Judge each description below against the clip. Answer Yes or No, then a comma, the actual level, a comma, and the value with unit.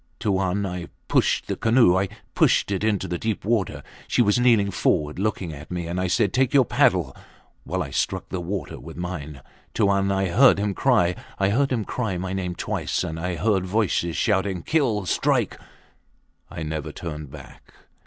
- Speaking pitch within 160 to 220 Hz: No, very low, 95 Hz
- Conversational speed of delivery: Yes, average, 180 wpm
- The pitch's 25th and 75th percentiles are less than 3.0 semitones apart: No, average, 3.4 semitones